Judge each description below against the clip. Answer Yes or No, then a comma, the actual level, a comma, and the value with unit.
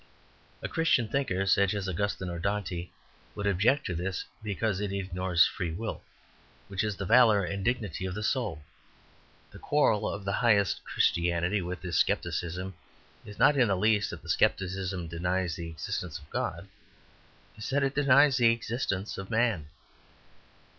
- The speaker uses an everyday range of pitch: Yes, average, 3.6 semitones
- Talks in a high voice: No, low, 100 Hz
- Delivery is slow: No, average, 165 wpm